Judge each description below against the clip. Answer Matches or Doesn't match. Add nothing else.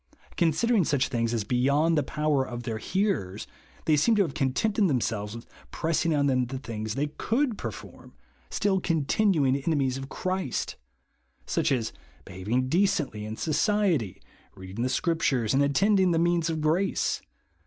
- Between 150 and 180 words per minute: Matches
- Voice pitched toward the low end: Doesn't match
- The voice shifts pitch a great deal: Matches